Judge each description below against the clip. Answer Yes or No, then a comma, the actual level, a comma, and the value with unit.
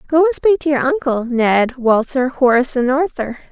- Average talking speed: Yes, average, 190 wpm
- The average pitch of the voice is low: No, very high, 270 Hz